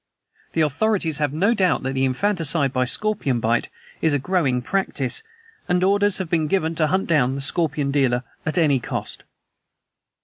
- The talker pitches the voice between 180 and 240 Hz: No, medium, 155 Hz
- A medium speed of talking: Yes, average, 165 wpm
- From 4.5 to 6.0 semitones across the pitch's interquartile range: Yes, wide, 5.4 semitones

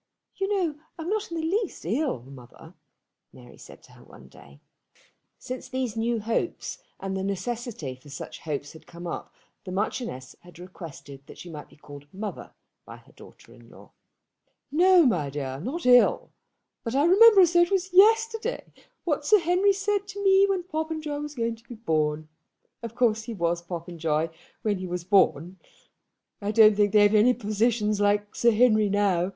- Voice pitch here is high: Yes, high, 220 Hz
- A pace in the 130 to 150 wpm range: No, average, 180 wpm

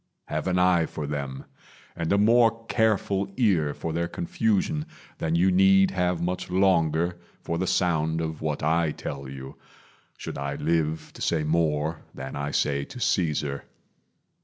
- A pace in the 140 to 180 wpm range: Yes, average, 160 wpm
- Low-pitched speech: Yes, very low, 85 Hz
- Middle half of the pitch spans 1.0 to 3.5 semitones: No, average, 3.9 semitones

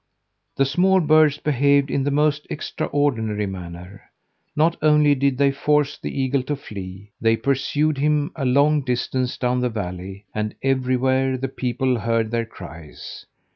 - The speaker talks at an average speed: Yes, average, 150 wpm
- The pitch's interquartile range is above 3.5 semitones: Yes, average, 4.4 semitones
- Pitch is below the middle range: Yes, low, 130 Hz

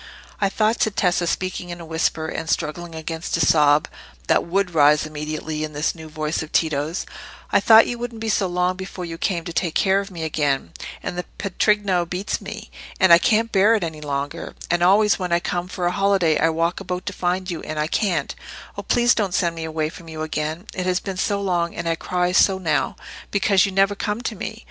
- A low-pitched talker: No, medium, 175 Hz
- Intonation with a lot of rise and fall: No, average, 3.5 semitones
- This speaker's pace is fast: Yes, fast, 225 wpm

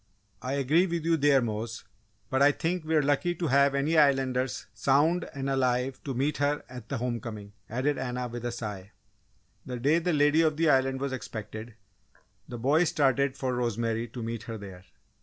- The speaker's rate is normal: Yes, average, 185 wpm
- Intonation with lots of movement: No, average, 3.5 semitones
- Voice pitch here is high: No, low, 130 Hz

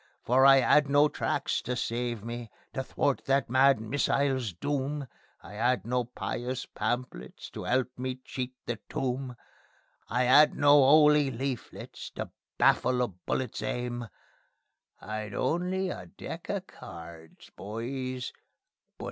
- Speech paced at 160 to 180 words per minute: No, average, 140 wpm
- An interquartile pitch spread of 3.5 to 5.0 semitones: No, average, 2.7 semitones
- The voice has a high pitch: No, low, 125 Hz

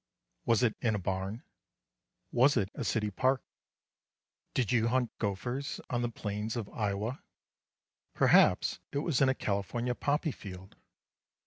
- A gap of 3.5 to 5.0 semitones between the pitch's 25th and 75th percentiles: Yes, average, 3.8 semitones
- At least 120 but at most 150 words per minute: Yes, average, 140 wpm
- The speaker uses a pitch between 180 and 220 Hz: No, low, 115 Hz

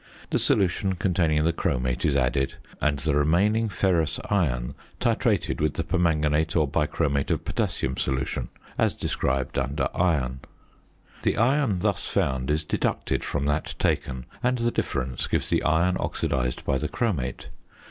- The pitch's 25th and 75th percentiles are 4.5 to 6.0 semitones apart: Yes, average, 4.9 semitones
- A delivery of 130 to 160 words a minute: Yes, average, 145 wpm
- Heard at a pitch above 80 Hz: No, very low, 75 Hz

